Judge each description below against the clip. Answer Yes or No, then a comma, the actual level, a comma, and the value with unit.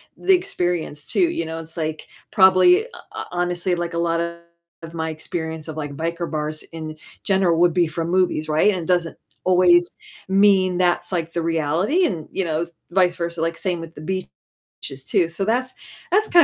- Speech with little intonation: Yes, narrow, 2.3 semitones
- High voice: No, medium, 170 Hz